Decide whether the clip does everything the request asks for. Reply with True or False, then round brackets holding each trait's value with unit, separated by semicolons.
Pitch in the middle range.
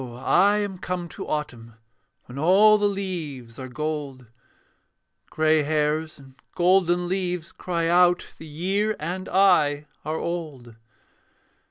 True (165 Hz)